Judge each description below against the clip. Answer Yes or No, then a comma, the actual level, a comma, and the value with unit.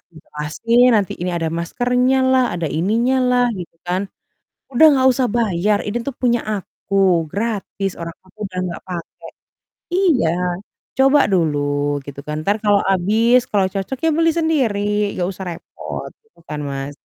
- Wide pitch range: Yes, wide, 6.5 semitones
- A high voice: Yes, high, 200 Hz